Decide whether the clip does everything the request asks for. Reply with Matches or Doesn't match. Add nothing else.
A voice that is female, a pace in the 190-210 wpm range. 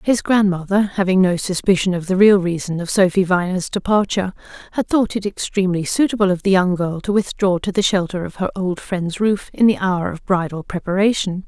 Matches